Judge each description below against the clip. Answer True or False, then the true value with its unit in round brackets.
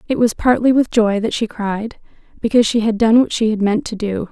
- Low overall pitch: False (220 Hz)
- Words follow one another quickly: True (235 wpm)